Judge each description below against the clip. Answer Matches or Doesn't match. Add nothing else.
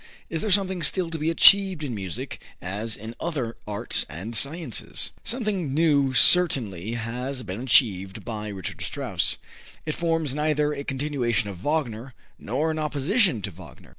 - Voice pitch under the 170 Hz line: Matches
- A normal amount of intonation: Doesn't match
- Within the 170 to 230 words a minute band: Doesn't match